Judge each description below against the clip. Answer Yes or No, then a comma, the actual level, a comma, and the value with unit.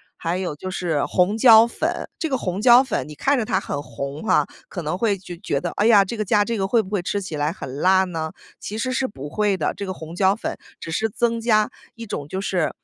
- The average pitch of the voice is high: Yes, high, 195 Hz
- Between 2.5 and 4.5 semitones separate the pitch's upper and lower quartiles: No, average, 5.0 semitones